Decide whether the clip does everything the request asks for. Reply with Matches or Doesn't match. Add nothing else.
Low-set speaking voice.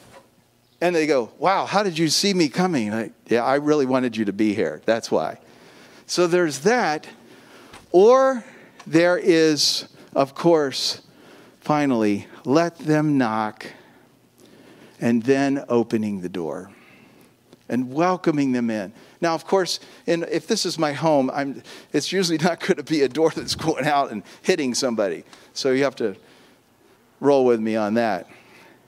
Doesn't match